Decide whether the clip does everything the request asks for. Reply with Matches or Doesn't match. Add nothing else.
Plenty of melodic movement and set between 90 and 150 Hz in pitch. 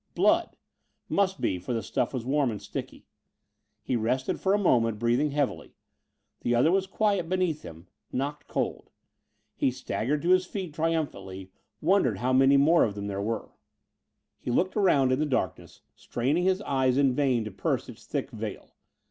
Matches